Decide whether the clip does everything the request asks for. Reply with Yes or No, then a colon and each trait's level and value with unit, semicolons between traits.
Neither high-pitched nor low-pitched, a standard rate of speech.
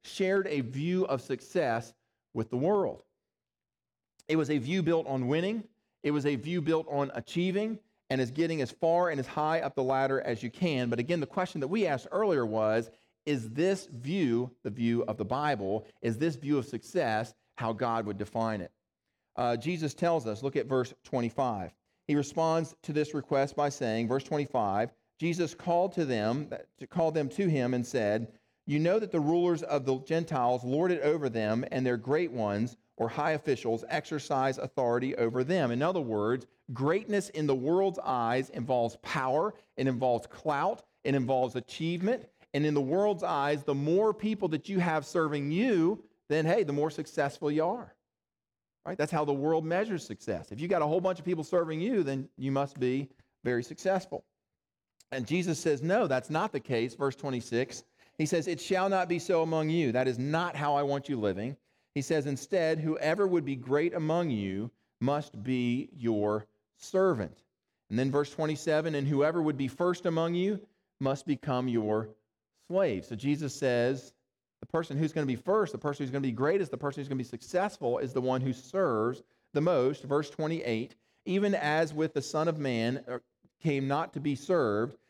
Yes: medium, 145 Hz; average, 190 wpm